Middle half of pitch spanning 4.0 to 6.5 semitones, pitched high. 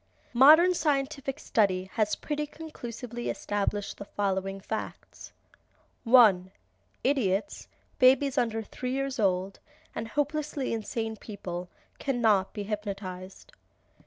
Yes: wide, 5.6 semitones; high, 225 Hz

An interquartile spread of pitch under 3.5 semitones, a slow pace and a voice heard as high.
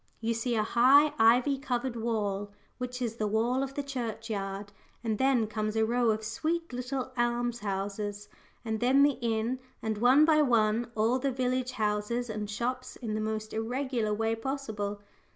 No: average, 2.9 semitones; average, 175 wpm; high, 230 Hz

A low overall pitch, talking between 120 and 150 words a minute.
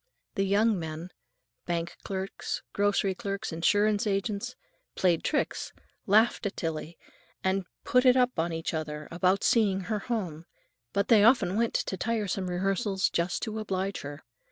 No: high, 195 Hz; average, 140 wpm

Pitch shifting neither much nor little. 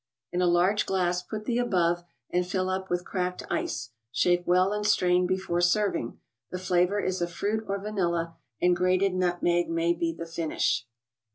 No: narrow, 1.7 semitones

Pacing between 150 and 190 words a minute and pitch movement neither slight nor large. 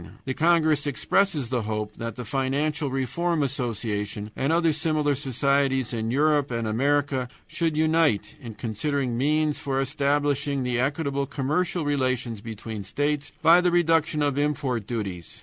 No: average, 140 wpm; average, 3.8 semitones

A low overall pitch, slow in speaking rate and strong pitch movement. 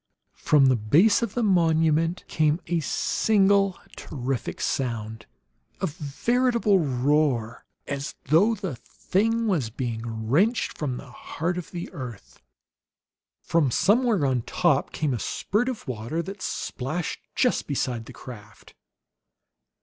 No: medium, 155 Hz; slow, 125 wpm; wide, 7.3 semitones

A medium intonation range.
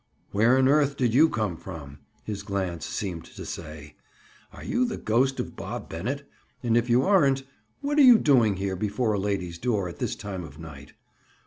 No: wide, 6.8 semitones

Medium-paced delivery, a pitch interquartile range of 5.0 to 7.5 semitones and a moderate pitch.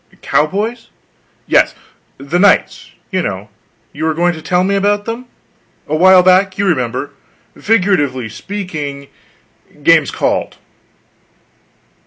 No: slow, 115 wpm; wide, 5.4 semitones; medium, 180 Hz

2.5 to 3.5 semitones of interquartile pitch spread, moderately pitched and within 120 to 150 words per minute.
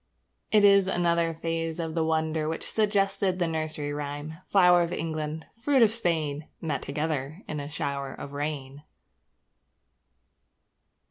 Yes: average, 2.9 semitones; medium, 160 Hz; slow, 135 wpm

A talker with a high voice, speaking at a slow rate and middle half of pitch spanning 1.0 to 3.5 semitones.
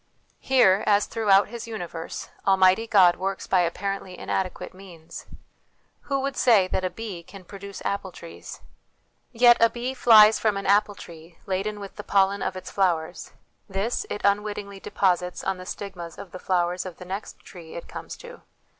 No: high, 195 Hz; average, 170 wpm; narrow, 2.4 semitones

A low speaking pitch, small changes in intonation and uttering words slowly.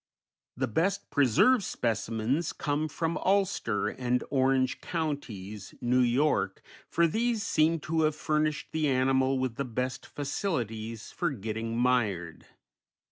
No: low, 130 Hz; average, 5.2 semitones; slow, 125 wpm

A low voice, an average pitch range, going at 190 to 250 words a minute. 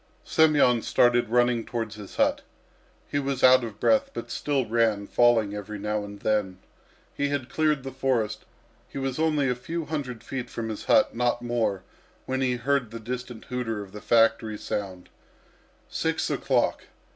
No: low, 120 Hz; average, 3.6 semitones; average, 170 wpm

